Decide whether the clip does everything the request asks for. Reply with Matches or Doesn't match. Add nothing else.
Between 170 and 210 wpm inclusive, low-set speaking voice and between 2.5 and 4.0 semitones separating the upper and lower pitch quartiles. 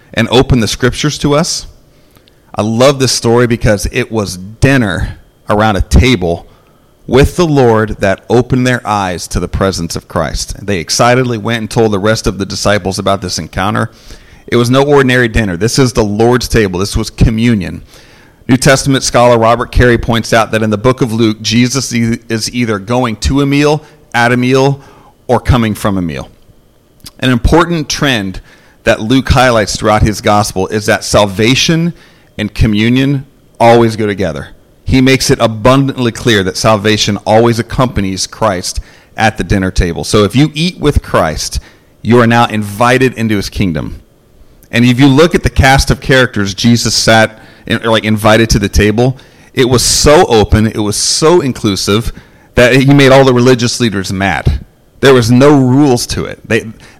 Matches